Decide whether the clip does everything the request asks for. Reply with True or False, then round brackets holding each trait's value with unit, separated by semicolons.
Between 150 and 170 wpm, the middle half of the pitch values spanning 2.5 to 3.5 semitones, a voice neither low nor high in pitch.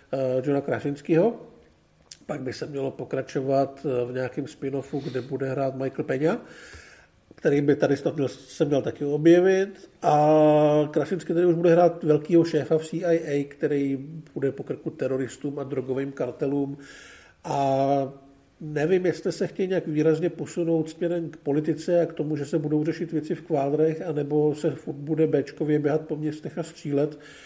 True (155 wpm; 2.8 semitones; 150 Hz)